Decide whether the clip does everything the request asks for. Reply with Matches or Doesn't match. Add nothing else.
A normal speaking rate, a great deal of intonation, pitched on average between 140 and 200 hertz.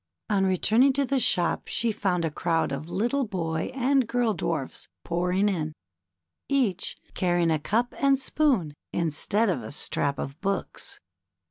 Matches